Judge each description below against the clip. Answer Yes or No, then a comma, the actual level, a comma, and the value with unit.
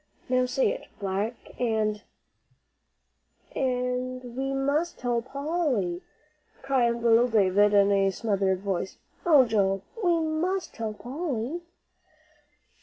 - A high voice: Yes, high, 245 Hz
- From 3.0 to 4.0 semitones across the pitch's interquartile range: No, average, 4.7 semitones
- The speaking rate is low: Yes, slow, 110 wpm